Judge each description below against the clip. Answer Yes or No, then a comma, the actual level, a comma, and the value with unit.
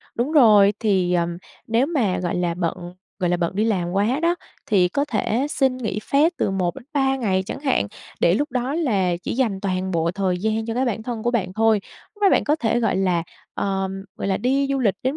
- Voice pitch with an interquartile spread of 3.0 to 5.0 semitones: No, wide, 5.6 semitones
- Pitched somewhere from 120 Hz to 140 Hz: No, high, 215 Hz